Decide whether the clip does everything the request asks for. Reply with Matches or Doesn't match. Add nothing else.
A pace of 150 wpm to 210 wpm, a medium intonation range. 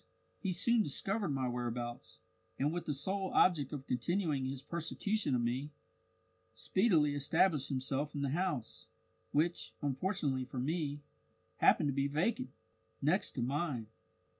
Doesn't match